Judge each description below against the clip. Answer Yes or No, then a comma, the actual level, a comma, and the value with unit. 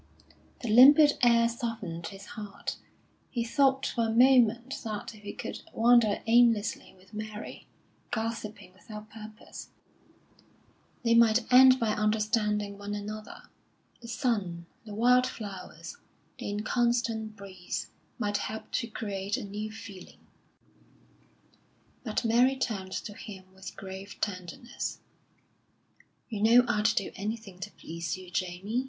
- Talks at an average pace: No, slow, 125 wpm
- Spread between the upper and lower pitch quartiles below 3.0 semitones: Yes, narrow, 2.6 semitones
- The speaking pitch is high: Yes, high, 215 Hz